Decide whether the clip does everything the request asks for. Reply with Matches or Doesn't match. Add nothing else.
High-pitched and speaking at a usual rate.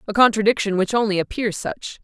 Matches